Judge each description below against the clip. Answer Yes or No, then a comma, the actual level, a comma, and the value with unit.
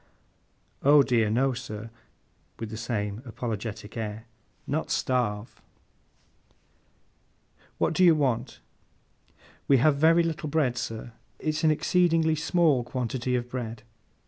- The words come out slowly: Yes, slow, 120 wpm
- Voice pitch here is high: No, low, 125 Hz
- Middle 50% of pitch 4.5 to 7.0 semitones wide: Yes, average, 5.3 semitones